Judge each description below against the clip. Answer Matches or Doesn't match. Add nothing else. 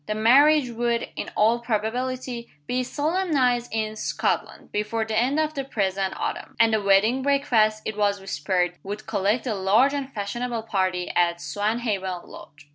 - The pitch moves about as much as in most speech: Matches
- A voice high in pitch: Matches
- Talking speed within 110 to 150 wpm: Doesn't match